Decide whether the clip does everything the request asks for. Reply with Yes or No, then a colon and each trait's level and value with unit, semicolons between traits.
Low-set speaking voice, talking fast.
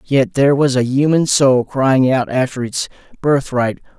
No: low, 130 Hz; average, 165 wpm